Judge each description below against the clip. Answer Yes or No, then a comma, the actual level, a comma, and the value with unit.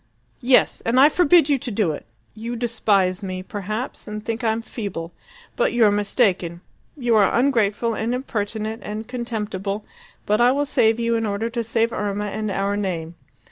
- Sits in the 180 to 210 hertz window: No, high, 220 Hz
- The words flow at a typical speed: Yes, average, 175 wpm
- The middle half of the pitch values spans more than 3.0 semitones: No, average, 2.7 semitones